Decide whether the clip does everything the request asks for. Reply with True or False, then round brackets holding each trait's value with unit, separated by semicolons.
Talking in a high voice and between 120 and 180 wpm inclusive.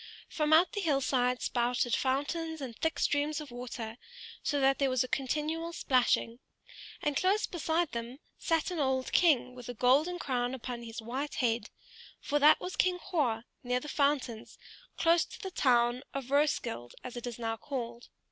True (265 Hz; 175 wpm)